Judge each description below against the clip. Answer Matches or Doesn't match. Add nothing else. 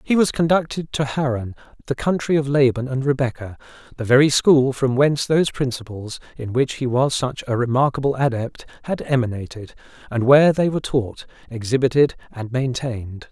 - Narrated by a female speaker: Doesn't match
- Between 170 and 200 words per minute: Doesn't match